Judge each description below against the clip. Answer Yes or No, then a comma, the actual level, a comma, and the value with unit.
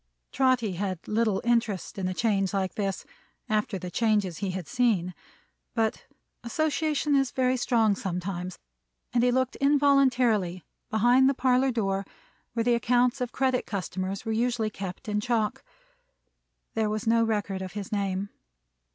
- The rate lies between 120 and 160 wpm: Yes, average, 150 wpm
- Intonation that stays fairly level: No, average, 4.2 semitones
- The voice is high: Yes, high, 220 Hz